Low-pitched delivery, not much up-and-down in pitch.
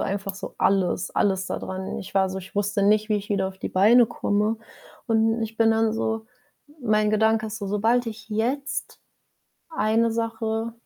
No: high, 215 Hz; narrow, 2.0 semitones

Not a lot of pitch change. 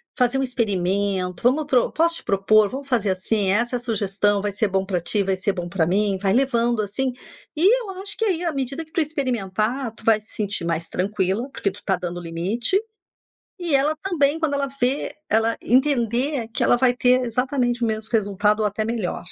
No: average, 5.1 semitones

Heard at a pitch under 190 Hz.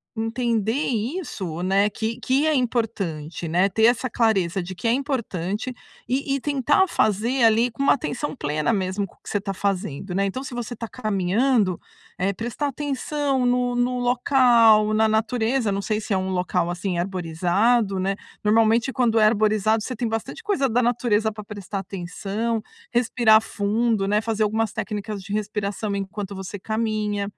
No: high, 220 Hz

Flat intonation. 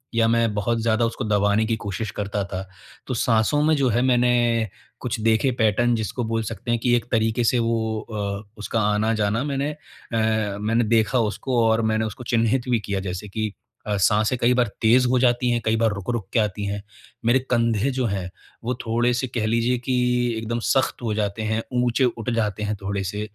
Yes: narrow, 2.2 semitones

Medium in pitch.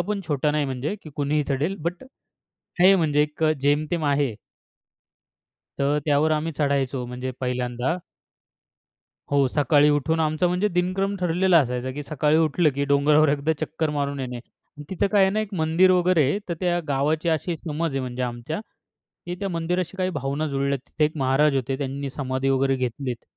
Yes: medium, 150 Hz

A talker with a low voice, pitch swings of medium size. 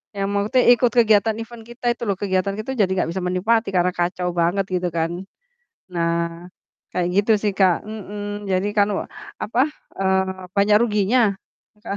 No: high, 200 Hz; average, 3.1 semitones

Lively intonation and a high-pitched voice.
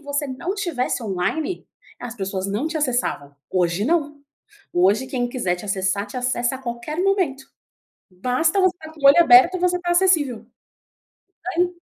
Yes: wide, 7.6 semitones; very high, 260 Hz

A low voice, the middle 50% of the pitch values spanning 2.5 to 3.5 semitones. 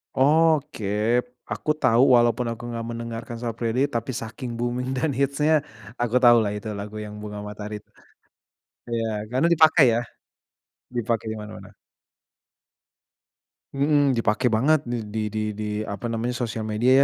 Yes: low, 120 Hz; average, 3.0 semitones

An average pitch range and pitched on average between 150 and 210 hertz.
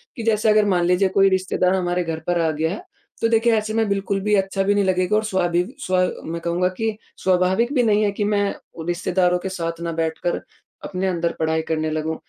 Yes: average, 3.1 semitones; medium, 185 Hz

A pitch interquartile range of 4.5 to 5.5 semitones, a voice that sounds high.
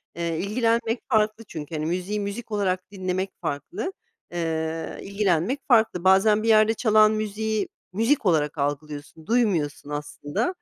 Yes: average, 5.2 semitones; high, 200 Hz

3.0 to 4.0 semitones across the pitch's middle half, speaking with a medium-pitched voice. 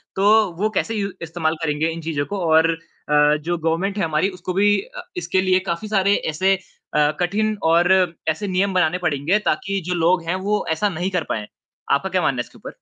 Yes: average, 3.6 semitones; medium, 180 Hz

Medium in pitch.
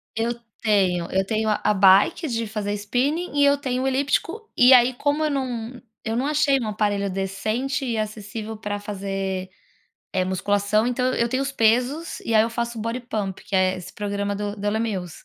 No: high, 220 Hz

